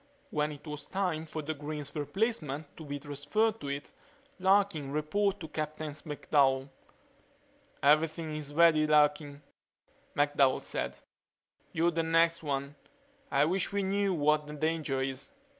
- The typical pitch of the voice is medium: Yes, medium, 155 Hz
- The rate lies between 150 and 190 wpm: No, slow, 135 wpm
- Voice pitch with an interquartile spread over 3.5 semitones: No, narrow, 2.4 semitones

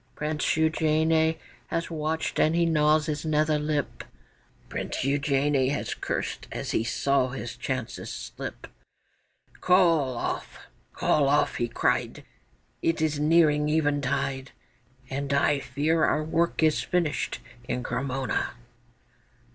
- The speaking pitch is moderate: Yes, medium, 150 Hz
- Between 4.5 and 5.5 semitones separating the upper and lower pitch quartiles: No, narrow, 2.4 semitones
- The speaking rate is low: Yes, slow, 120 wpm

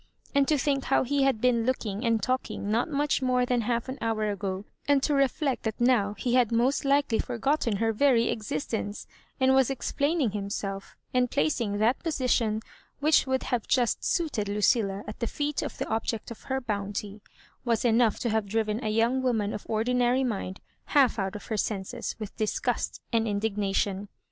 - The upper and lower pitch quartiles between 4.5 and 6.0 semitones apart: No, average, 3.7 semitones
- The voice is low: No, high, 230 Hz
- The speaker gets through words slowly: No, average, 185 wpm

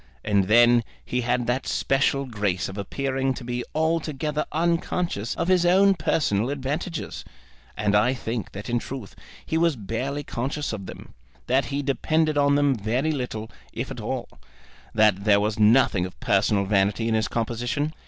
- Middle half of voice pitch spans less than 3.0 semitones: No, average, 5.1 semitones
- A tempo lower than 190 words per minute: Yes, average, 165 wpm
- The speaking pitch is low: Yes, low, 125 Hz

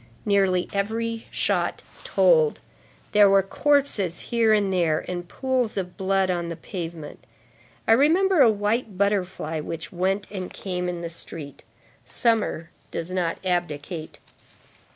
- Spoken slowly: Yes, slow, 130 wpm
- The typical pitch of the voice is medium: No, high, 195 Hz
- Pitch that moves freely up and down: No, average, 4.2 semitones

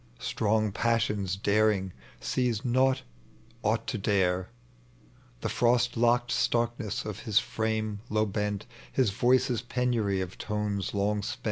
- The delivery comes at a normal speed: No, slow, 125 wpm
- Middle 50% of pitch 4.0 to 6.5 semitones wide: No, average, 2.8 semitones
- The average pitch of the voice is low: Yes, low, 110 Hz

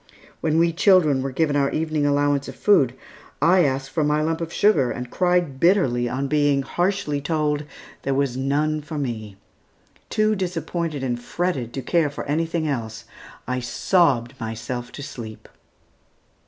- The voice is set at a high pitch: No, medium, 145 Hz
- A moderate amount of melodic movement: Yes, average, 3.9 semitones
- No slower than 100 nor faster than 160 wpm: Yes, average, 155 wpm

